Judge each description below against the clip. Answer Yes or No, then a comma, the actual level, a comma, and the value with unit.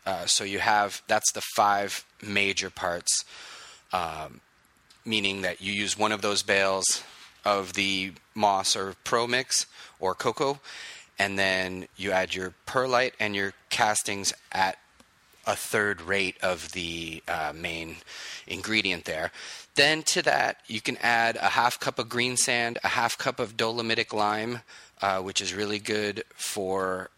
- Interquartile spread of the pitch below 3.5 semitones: Yes, average, 3.0 semitones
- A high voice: No, low, 100 Hz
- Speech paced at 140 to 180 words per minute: Yes, average, 150 wpm